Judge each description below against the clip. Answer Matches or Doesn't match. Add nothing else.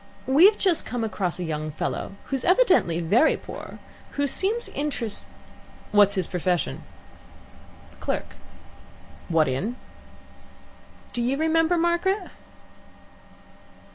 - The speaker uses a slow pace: Matches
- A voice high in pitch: Matches